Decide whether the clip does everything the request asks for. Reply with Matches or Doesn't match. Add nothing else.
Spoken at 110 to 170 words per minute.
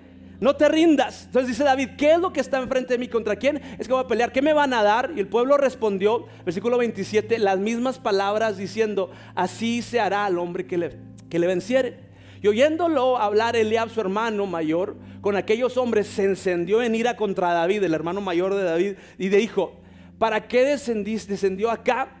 Doesn't match